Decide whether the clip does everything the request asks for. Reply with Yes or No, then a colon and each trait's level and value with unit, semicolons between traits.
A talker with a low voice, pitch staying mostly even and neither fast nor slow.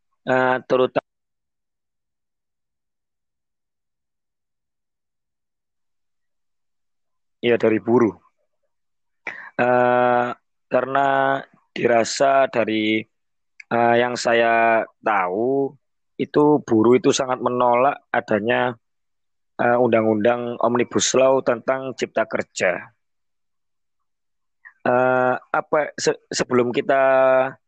No: low, 125 Hz; narrow, 2.1 semitones; slow, 65 wpm